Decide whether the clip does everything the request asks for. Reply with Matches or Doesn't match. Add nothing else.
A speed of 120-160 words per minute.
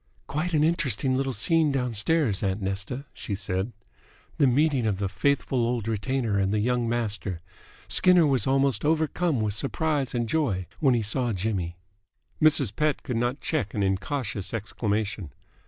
Matches